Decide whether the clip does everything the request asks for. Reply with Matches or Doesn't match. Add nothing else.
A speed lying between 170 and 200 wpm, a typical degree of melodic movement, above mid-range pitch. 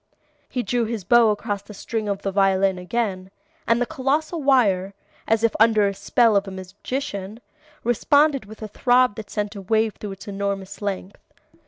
Matches